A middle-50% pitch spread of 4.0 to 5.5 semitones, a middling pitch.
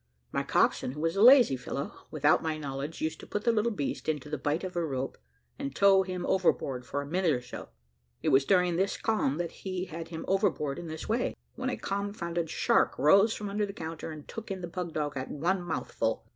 Yes: average, 4.7 semitones; medium, 170 Hz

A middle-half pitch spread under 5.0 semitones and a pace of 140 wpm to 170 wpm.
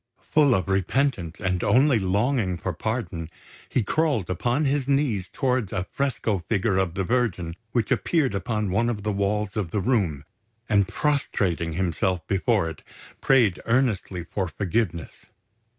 No: average, 5.3 semitones; average, 150 wpm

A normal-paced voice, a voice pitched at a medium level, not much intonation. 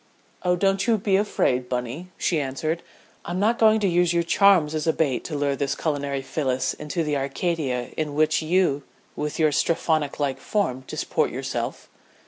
No: average, 170 wpm; medium, 155 Hz; average, 4.2 semitones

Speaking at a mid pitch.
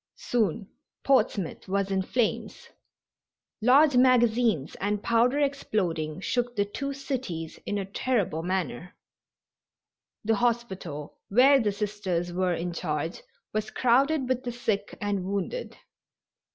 No: high, 210 Hz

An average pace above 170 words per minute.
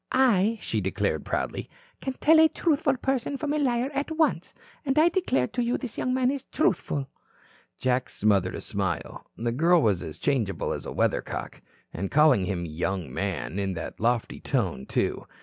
Yes: average, 180 wpm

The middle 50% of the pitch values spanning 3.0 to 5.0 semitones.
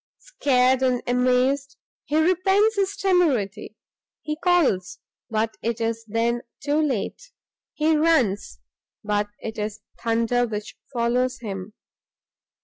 No: wide, 5.6 semitones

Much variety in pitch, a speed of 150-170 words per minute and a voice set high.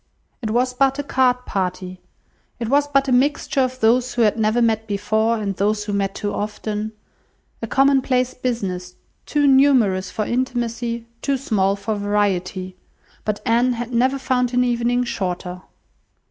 No: average, 3.6 semitones; average, 160 wpm; high, 230 Hz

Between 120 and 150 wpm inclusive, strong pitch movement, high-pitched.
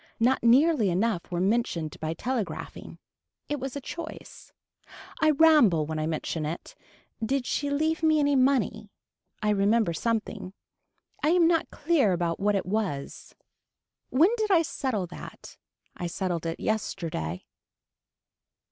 Yes: average, 140 wpm; wide, 8.5 semitones; high, 220 Hz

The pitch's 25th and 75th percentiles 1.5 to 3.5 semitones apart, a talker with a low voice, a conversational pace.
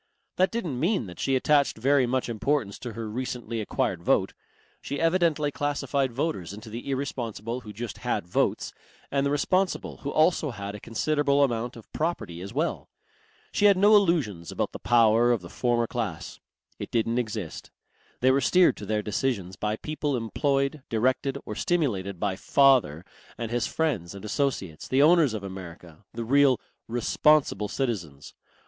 No: average, 5.2 semitones; low, 120 Hz; average, 165 wpm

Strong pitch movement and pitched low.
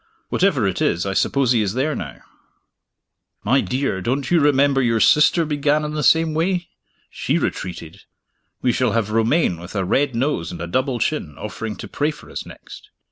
Yes: wide, 6.6 semitones; low, 130 Hz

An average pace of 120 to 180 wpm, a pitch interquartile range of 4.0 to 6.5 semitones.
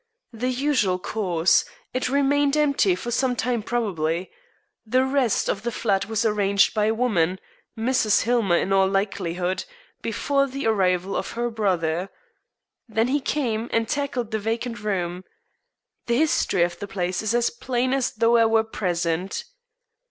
Yes: average, 155 wpm; average, 4.6 semitones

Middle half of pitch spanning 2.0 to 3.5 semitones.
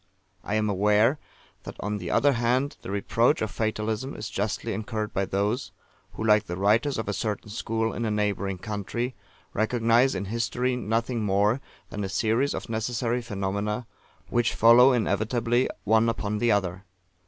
Yes: narrow, 2.4 semitones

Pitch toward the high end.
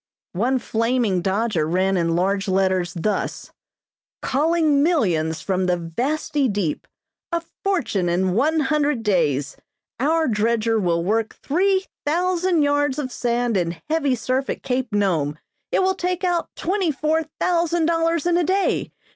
Yes: very high, 250 Hz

